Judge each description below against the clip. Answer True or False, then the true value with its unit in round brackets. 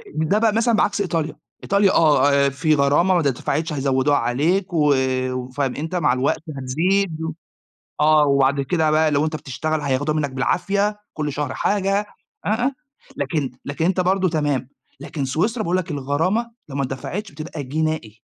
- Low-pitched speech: False (155 Hz)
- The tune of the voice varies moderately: True (4.7 semitones)